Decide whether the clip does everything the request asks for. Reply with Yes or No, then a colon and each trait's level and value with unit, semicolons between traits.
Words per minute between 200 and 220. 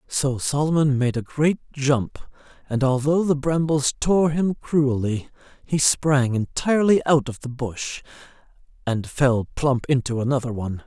No: average, 145 wpm